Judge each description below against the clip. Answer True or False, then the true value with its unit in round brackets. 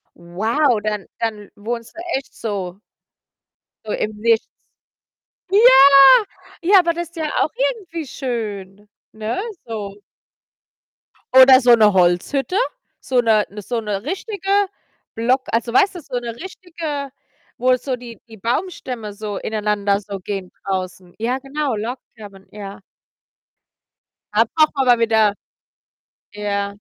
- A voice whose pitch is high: True (230 Hz)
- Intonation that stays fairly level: False (5.1 semitones)